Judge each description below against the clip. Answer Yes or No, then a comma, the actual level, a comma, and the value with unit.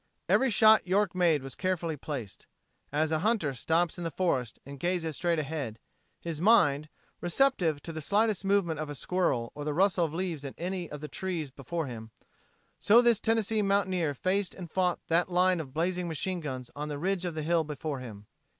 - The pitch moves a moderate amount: Yes, average, 4.0 semitones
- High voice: No, medium, 170 Hz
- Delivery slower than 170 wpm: No, average, 195 wpm